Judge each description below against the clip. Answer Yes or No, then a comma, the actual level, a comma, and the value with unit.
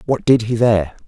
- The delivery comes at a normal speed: No, fast, 225 wpm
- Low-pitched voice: Yes, low, 110 Hz